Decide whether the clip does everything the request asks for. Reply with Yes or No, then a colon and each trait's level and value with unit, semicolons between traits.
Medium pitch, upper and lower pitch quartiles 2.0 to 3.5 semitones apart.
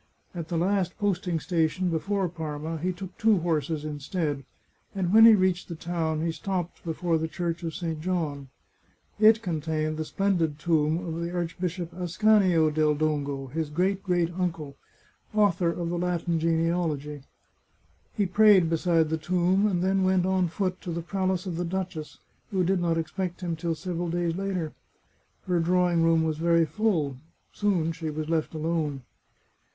Yes: medium, 170 Hz; narrow, 2.4 semitones